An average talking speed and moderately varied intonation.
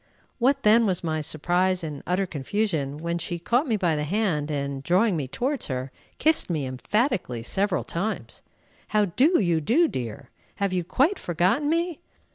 No: average, 170 wpm; wide, 6.8 semitones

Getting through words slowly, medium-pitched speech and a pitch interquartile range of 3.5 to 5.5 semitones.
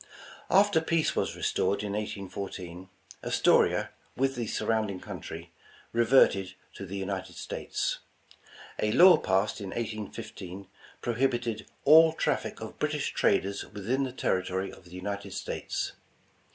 No: slow, 125 wpm; low, 105 Hz; average, 4.3 semitones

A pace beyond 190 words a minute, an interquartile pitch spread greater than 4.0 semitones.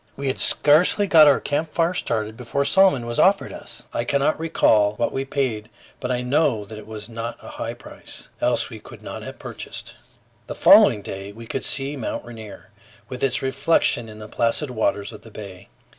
Yes: average, 200 wpm; average, 4.7 semitones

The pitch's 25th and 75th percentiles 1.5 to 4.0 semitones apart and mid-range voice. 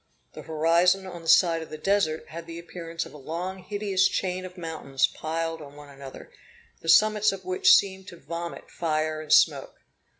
Yes: average, 2.9 semitones; medium, 170 Hz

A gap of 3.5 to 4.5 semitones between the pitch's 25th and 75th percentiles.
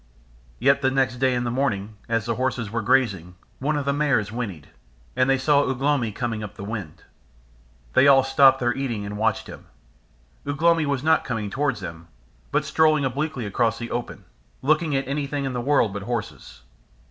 Yes: average, 4.0 semitones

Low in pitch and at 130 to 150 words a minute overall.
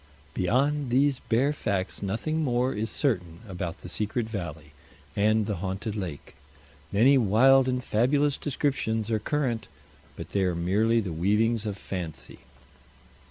Yes: low, 110 Hz; average, 140 wpm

